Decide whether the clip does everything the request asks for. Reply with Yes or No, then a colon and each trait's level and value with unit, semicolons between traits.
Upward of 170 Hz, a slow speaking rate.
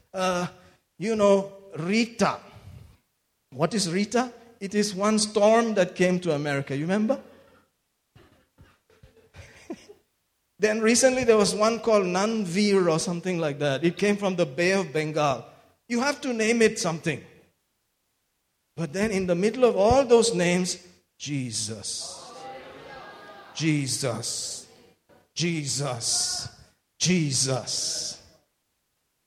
Yes: medium, 185 Hz; slow, 115 wpm